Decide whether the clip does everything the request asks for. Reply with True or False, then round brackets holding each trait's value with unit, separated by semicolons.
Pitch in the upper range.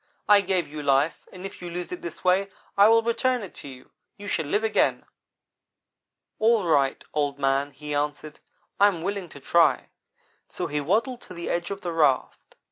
False (175 Hz)